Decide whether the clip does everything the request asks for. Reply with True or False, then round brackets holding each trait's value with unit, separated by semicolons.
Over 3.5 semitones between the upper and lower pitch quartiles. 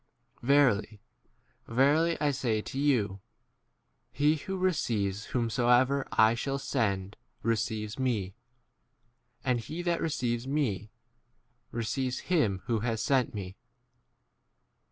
True (4.6 semitones)